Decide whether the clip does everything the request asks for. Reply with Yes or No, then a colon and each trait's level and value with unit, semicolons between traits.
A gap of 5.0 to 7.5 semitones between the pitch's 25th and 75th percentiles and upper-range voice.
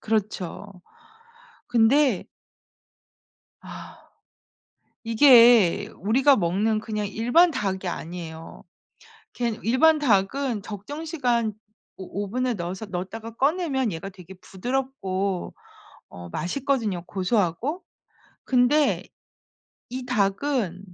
Yes: average, 5.3 semitones; high, 220 Hz